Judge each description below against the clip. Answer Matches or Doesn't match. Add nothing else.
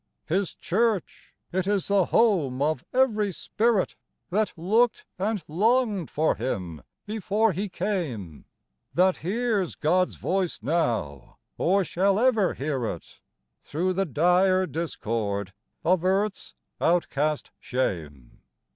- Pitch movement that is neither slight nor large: Doesn't match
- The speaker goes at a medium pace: Doesn't match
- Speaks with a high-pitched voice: Doesn't match